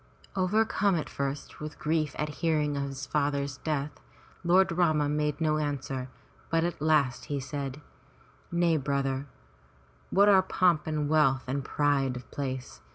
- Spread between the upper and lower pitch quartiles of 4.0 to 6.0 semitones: No, narrow, 2.5 semitones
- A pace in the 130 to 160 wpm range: Yes, average, 150 wpm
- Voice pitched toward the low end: No, medium, 150 Hz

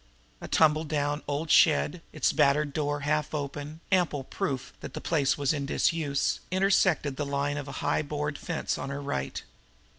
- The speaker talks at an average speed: Yes, average, 170 wpm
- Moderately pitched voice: Yes, medium, 145 Hz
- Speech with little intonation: Yes, narrow, 1.7 semitones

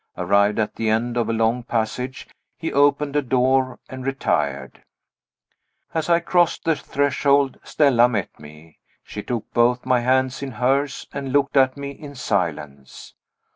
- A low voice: Yes, low, 130 Hz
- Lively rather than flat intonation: No, average, 3.9 semitones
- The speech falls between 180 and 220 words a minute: No, average, 155 wpm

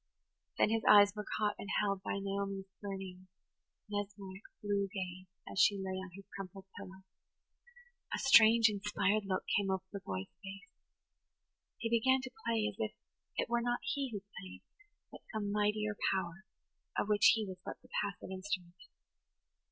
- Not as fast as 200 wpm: Yes, average, 160 wpm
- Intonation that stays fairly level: Yes, narrow, 1.9 semitones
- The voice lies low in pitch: No, high, 200 Hz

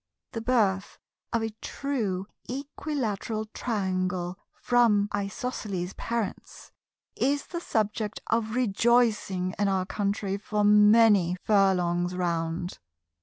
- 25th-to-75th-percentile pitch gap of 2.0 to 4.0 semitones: Yes, average, 3.6 semitones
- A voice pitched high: Yes, high, 205 Hz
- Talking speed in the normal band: No, slow, 100 wpm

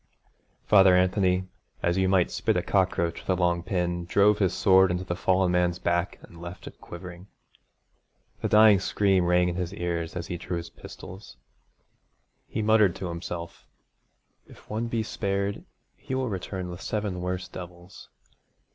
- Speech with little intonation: Yes, narrow, 2.0 semitones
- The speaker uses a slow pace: No, average, 165 wpm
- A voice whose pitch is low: Yes, very low, 90 Hz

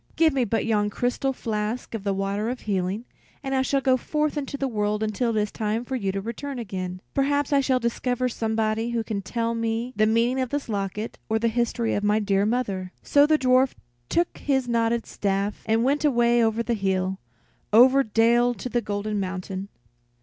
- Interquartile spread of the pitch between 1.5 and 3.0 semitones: No, average, 3.5 semitones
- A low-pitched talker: No, high, 230 Hz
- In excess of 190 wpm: Yes, average, 200 wpm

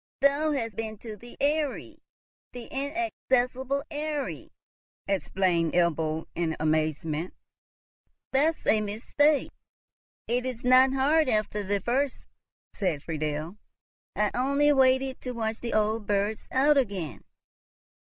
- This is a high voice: Yes, high, 235 Hz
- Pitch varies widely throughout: Yes, wide, 6.2 semitones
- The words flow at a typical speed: No, slow, 110 wpm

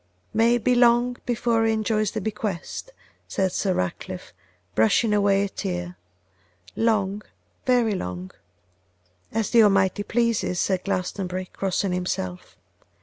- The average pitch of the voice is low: No, high, 200 Hz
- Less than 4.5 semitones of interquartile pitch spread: Yes, average, 4.1 semitones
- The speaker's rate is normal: No, slow, 125 wpm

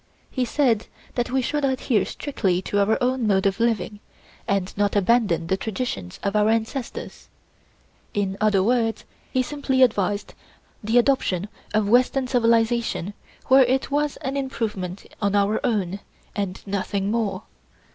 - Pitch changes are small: No, average, 4.0 semitones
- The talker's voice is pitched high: Yes, high, 220 Hz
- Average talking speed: Yes, average, 145 wpm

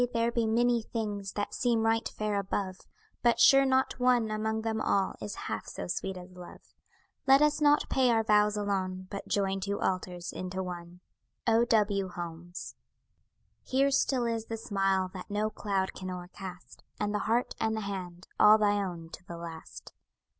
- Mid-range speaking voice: No, high, 205 Hz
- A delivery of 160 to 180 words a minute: Yes, average, 175 wpm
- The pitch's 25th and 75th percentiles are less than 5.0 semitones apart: Yes, average, 3.4 semitones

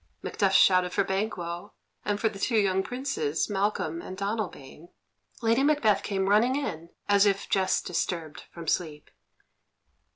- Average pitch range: Yes, average, 3.6 semitones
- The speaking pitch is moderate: No, high, 195 Hz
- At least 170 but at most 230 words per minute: No, average, 140 wpm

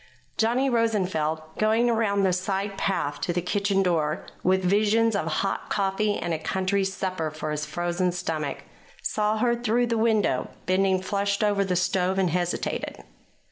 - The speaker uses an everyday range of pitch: Yes, average, 3.2 semitones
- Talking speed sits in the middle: Yes, average, 160 wpm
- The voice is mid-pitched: No, high, 195 Hz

